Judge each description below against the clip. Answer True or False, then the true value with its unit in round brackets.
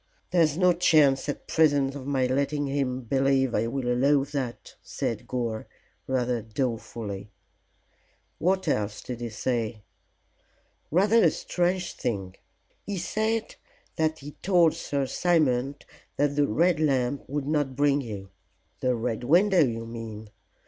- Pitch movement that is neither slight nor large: True (4.6 semitones)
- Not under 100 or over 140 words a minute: True (135 wpm)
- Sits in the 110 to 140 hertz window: True (135 Hz)